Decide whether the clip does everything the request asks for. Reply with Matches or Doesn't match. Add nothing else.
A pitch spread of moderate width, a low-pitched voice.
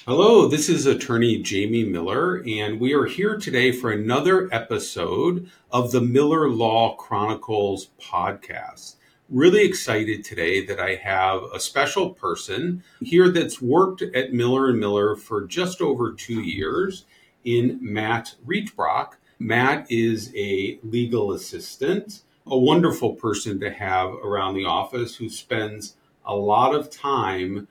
Doesn't match